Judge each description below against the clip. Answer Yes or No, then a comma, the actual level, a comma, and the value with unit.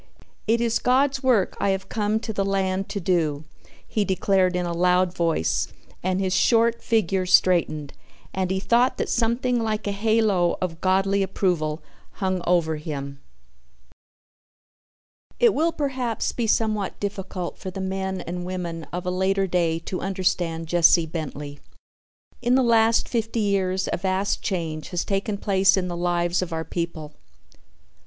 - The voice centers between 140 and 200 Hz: Yes, high, 190 Hz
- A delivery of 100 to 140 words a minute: No, average, 155 wpm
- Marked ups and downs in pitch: No, average, 3.4 semitones